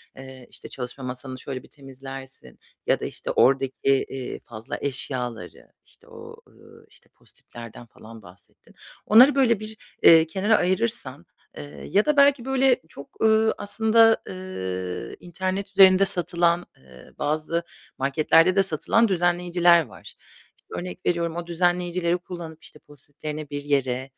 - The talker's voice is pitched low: No, medium, 165 Hz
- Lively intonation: Yes, wide, 6.1 semitones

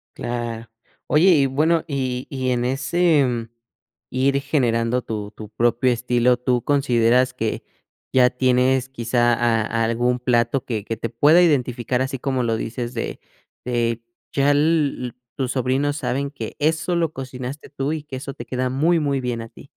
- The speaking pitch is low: Yes, low, 125 Hz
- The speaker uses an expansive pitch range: No, average, 2.7 semitones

